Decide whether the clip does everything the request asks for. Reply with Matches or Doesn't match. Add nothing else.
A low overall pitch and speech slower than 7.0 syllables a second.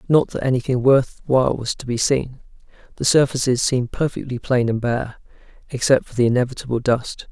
Matches